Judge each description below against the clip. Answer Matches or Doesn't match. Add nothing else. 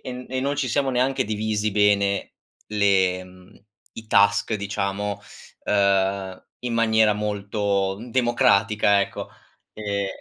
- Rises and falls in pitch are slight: Matches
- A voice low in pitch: Matches